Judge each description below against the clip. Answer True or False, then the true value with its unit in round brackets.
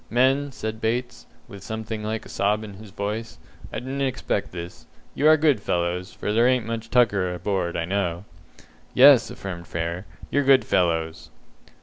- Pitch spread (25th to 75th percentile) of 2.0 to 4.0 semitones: False (5.1 semitones)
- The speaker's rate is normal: True (165 wpm)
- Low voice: True (110 Hz)